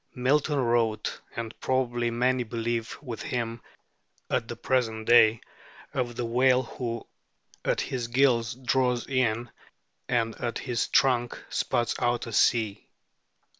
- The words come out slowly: Yes, slow, 130 wpm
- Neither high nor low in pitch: No, low, 120 Hz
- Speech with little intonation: Yes, narrow, 1.7 semitones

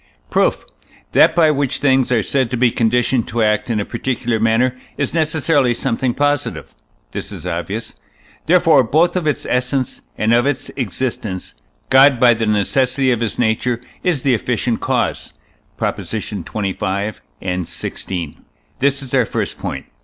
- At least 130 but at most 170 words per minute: Yes, average, 155 wpm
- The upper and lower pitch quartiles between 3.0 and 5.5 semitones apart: Yes, average, 3.7 semitones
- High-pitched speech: No, low, 125 Hz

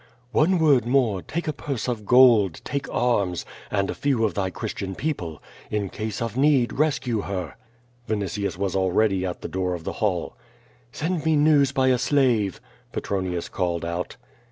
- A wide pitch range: Yes, wide, 6.3 semitones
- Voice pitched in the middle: No, low, 110 Hz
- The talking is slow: No, average, 170 wpm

